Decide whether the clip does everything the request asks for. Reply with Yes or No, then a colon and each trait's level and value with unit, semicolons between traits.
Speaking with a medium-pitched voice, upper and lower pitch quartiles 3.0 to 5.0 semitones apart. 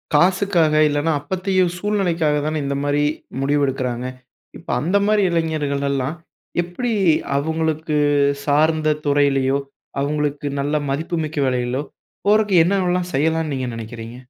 Yes: medium, 150 Hz; average, 3.6 semitones